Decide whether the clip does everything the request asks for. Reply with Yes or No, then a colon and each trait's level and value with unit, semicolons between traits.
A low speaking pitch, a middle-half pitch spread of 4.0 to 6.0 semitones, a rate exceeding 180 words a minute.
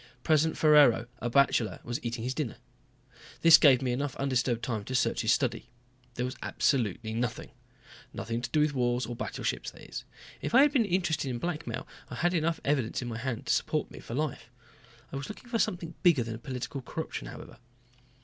Yes: low, 130 Hz; average, 4.6 semitones; average, 195 wpm